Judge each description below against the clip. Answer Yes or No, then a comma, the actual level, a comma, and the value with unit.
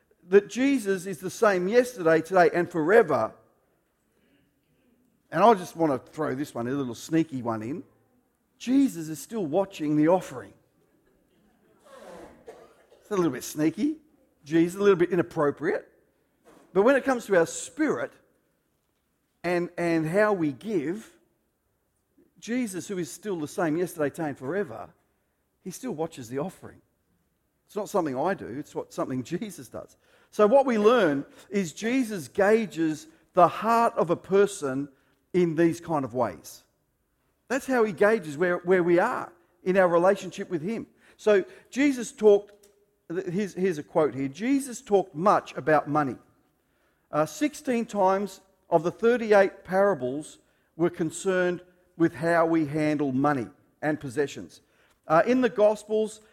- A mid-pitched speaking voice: Yes, medium, 180 Hz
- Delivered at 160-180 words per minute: No, average, 145 wpm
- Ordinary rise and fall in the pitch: Yes, average, 5.0 semitones